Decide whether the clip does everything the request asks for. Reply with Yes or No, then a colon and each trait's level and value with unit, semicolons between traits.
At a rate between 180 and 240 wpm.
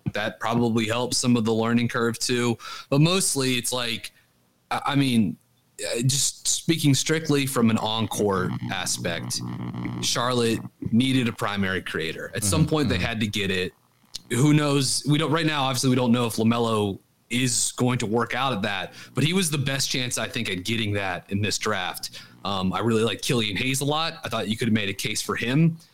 Yes: average, 200 wpm